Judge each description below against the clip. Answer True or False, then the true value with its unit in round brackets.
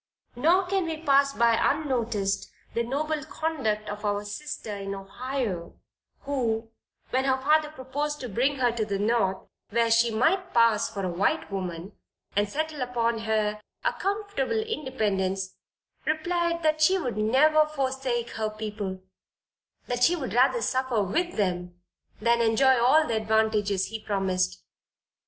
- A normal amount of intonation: False (6.0 semitones)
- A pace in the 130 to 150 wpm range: True (145 wpm)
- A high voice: True (235 Hz)